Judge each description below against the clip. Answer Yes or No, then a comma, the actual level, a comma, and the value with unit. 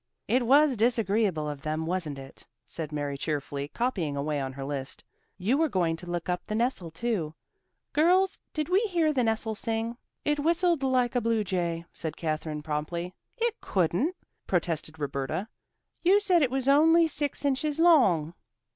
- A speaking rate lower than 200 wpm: Yes, average, 165 wpm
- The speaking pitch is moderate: No, high, 210 Hz